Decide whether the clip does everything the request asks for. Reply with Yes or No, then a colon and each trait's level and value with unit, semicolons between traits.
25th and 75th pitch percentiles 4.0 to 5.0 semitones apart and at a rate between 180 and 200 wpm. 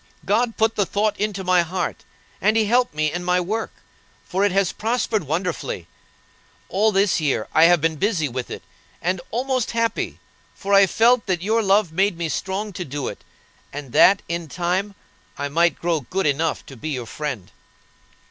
Yes: average, 4.6 semitones; average, 185 wpm